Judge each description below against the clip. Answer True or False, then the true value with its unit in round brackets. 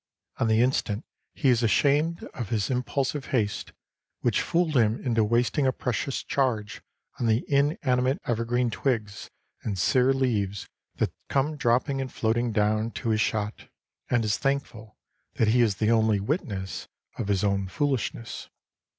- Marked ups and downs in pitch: False (3.7 semitones)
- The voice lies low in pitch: True (115 Hz)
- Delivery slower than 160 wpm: True (150 wpm)